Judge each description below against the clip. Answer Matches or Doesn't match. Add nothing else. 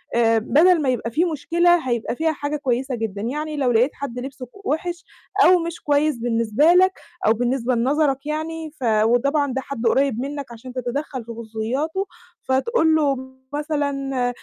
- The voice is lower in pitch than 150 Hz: Doesn't match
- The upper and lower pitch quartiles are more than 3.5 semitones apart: Matches